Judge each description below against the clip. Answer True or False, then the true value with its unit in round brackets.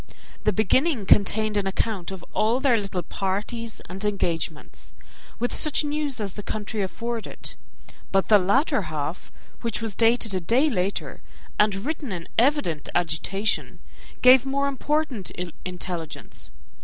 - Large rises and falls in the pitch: False (4.8 semitones)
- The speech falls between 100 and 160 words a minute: True (135 wpm)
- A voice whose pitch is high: True (210 Hz)